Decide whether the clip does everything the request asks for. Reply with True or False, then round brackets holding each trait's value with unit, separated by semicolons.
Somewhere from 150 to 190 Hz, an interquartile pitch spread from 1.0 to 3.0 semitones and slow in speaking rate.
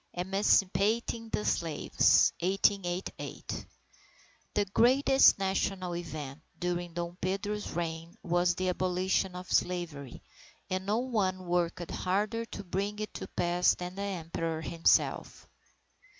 True (185 Hz; 2.5 semitones; 120 wpm)